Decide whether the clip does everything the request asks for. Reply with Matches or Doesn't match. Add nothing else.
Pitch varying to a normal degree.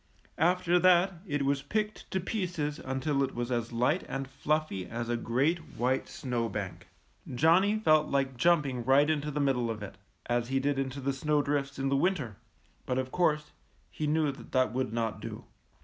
Matches